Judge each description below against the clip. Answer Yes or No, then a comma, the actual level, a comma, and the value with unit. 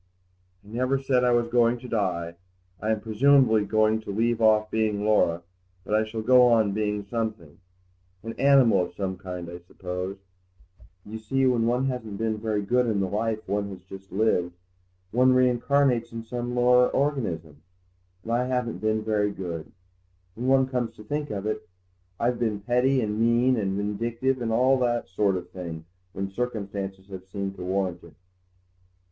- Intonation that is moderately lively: Yes, average, 3.8 semitones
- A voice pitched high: No, low, 110 Hz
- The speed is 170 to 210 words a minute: Yes, average, 175 wpm